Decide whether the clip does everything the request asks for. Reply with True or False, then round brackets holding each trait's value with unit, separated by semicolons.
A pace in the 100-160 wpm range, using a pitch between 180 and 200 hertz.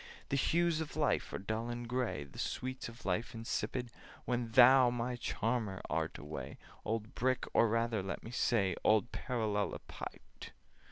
False (155 wpm; 115 Hz)